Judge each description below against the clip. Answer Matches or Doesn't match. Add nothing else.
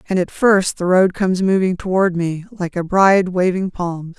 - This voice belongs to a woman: Matches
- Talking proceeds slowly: Doesn't match